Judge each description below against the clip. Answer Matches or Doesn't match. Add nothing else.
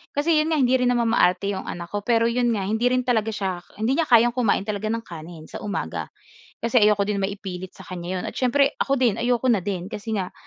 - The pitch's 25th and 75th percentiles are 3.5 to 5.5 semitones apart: Matches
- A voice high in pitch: Matches